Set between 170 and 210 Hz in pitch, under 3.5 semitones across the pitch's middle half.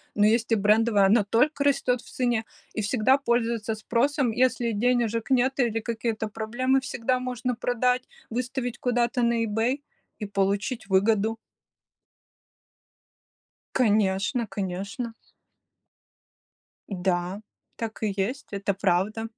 No: high, 230 Hz; average, 3.1 semitones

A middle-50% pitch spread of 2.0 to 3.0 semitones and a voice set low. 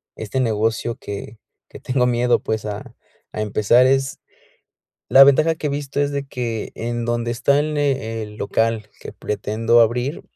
No: average, 3.6 semitones; low, 120 Hz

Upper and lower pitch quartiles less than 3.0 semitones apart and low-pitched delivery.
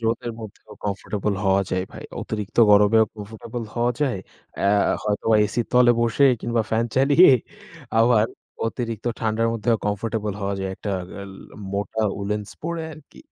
Yes: narrow, 2.5 semitones; low, 110 Hz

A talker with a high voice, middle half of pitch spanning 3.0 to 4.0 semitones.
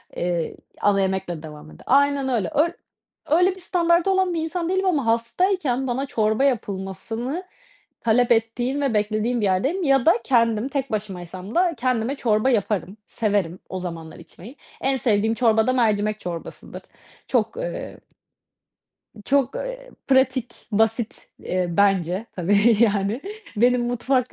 No: high, 235 Hz; average, 5.1 semitones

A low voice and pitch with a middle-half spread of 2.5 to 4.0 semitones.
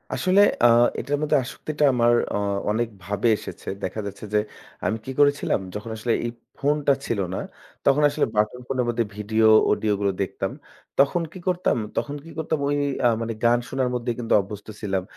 No: low, 120 Hz; average, 5.2 semitones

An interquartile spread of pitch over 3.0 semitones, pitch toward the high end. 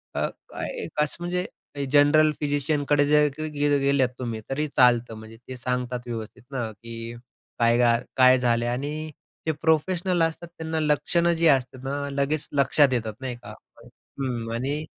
No: average, 3.8 semitones; medium, 140 Hz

